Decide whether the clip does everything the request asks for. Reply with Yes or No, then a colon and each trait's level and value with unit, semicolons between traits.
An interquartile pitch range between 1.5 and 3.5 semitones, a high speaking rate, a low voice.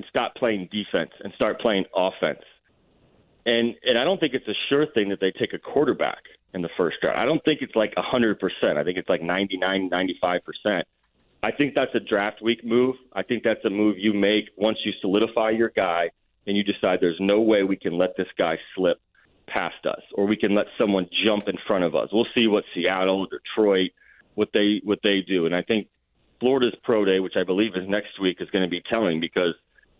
Yes: average, 2.9 semitones; fast, 220 wpm; low, 105 Hz